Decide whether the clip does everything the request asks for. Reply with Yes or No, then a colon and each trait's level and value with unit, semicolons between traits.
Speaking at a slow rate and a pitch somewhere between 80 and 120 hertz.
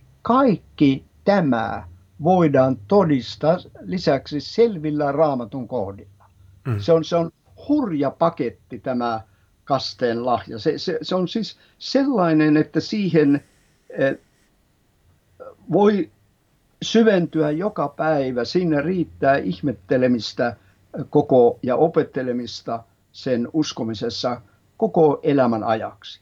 No: slow, 90 wpm; medium, 140 Hz